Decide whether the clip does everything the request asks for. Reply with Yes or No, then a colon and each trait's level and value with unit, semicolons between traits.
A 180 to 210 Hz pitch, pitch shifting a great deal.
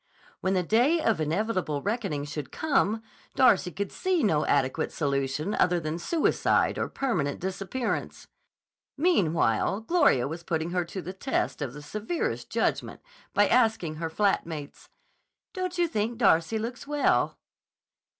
Yes: high, 190 Hz; wide, 7.1 semitones